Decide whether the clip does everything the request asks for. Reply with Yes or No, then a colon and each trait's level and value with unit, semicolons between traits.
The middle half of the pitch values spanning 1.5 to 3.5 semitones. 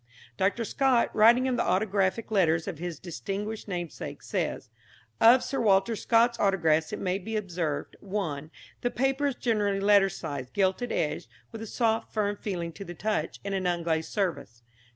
No: average, 4.3 semitones